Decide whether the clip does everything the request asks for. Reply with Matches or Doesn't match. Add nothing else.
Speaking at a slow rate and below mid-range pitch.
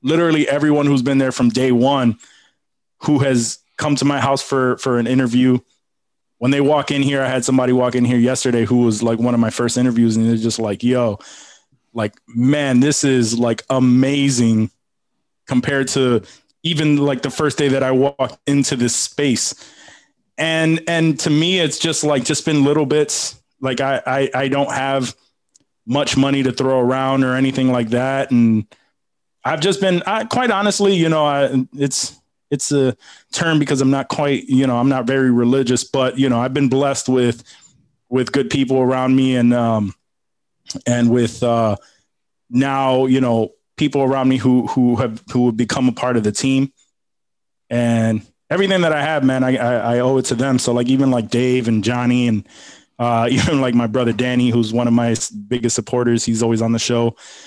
Doesn't match